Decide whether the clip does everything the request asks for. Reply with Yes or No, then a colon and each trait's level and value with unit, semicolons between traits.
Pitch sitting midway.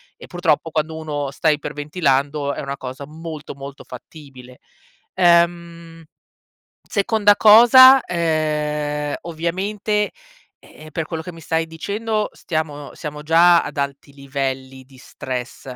Yes: medium, 155 Hz